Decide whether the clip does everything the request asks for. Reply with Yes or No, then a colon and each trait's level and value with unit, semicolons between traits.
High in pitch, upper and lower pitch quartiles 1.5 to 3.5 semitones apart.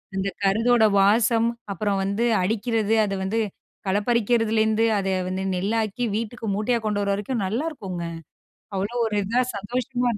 Yes: high, 215 Hz; average, 2.8 semitones